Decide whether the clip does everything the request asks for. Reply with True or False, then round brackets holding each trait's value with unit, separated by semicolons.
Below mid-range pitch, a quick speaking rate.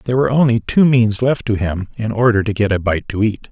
True (110 Hz; 275 wpm)